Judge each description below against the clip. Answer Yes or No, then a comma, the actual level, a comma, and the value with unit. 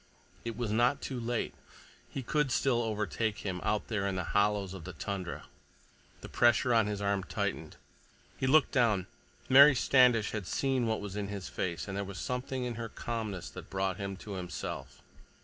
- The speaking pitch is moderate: No, low, 105 Hz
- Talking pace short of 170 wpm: No, average, 185 wpm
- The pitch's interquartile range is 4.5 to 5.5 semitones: No, average, 3.7 semitones